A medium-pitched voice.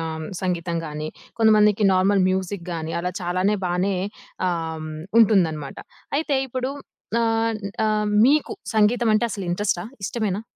No: high, 195 Hz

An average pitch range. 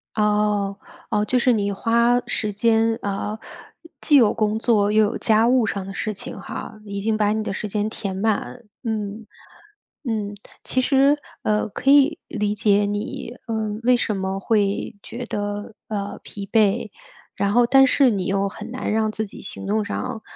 No: narrow, 2.1 semitones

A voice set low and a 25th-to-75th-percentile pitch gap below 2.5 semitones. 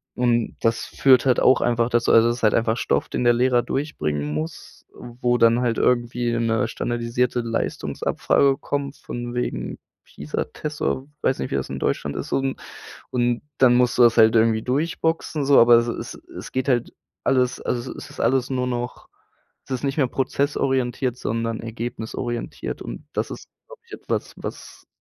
Yes: low, 120 Hz; narrow, 2.0 semitones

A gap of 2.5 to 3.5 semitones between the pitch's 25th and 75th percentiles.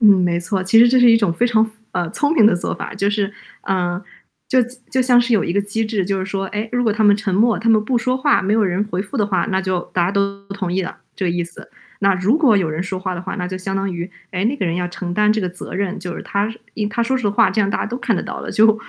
Yes: average, 3.2 semitones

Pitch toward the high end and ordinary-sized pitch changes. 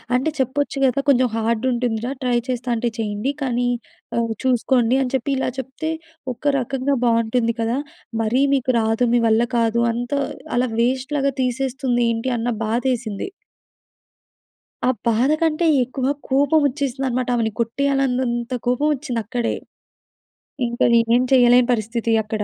No: high, 245 Hz; narrow, 2.3 semitones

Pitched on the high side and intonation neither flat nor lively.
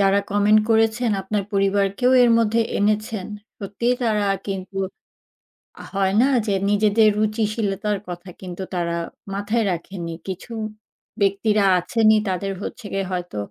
No: high, 205 Hz; narrow, 2.0 semitones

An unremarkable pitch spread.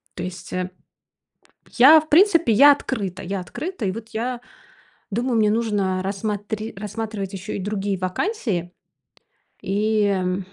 Yes: average, 3.7 semitones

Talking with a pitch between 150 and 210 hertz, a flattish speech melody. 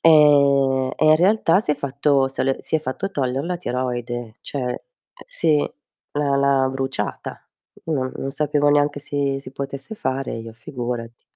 No: medium, 140 Hz; narrow, 2.3 semitones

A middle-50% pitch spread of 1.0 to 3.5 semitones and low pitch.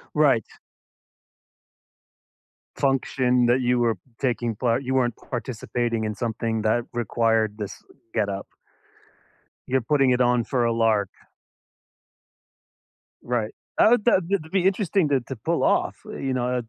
Yes: average, 2.8 semitones; low, 120 Hz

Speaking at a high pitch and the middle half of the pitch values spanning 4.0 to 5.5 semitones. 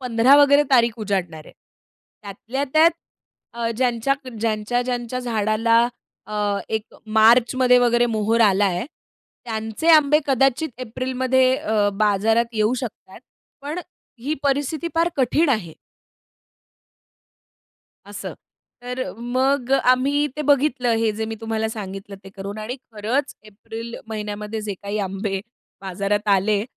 No: high, 230 Hz; average, 3.5 semitones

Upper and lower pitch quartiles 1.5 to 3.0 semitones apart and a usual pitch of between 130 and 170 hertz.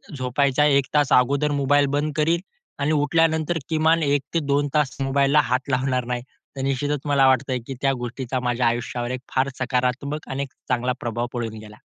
Yes: narrow, 2.4 semitones; low, 135 Hz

